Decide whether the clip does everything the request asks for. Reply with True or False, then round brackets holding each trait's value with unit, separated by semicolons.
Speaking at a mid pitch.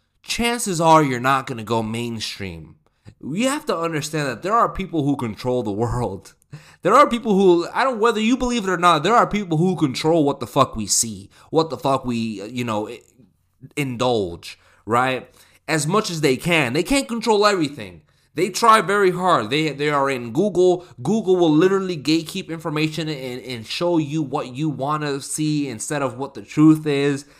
True (155 Hz)